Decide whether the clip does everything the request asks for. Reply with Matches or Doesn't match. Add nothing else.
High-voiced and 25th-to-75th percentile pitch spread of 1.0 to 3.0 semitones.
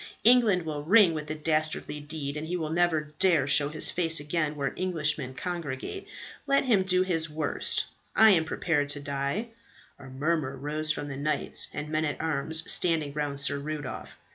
Doesn't match